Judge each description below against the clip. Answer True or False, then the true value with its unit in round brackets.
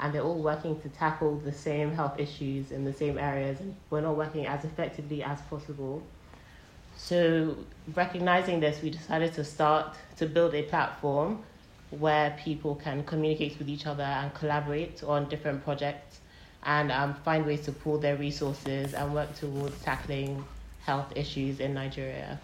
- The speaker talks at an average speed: True (160 wpm)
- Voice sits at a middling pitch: True (150 Hz)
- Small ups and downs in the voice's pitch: True (1.5 semitones)